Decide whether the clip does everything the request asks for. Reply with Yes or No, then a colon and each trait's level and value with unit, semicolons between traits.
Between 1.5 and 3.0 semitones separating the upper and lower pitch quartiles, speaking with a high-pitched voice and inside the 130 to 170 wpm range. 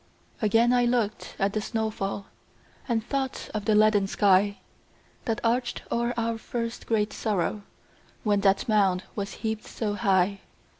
Yes: narrow, 2.5 semitones; high, 215 Hz; average, 150 wpm